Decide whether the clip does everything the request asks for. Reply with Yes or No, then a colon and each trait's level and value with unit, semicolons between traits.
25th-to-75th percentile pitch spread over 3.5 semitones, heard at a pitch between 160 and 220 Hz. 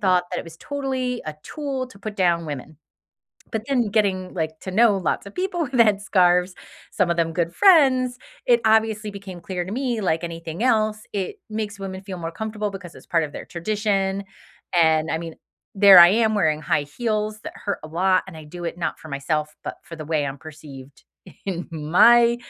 Yes: average, 4.7 semitones; high, 190 Hz